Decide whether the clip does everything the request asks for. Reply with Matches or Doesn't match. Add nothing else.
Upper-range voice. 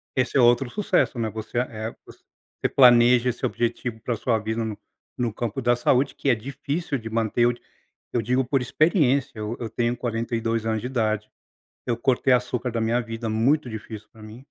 Doesn't match